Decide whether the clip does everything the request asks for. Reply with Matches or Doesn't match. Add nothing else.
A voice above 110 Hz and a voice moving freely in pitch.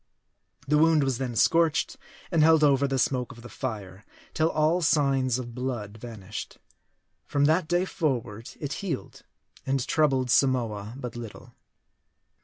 Doesn't match